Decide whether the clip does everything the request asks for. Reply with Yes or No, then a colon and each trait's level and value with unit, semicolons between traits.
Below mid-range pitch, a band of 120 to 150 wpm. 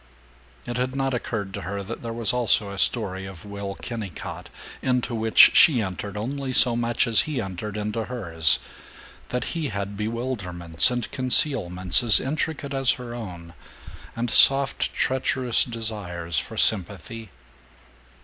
Yes: low, 115 Hz; average, 145 wpm